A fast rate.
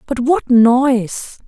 No: slow, 120 wpm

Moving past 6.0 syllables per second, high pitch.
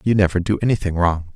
No: 6.4 syllables/s; very low, 95 Hz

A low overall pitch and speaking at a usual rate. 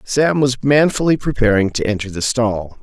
Yes: low, 125 Hz; average, 170 wpm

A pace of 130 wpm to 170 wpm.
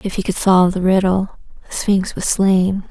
No: fast, 205 wpm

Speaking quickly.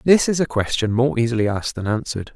Yes: fast, 230 wpm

